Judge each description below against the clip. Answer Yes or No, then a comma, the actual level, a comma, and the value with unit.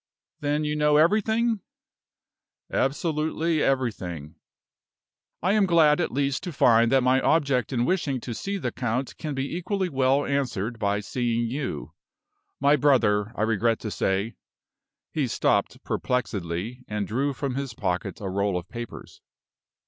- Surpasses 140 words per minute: Yes, average, 150 wpm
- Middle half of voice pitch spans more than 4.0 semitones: Yes, average, 5.0 semitones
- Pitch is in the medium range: No, low, 130 Hz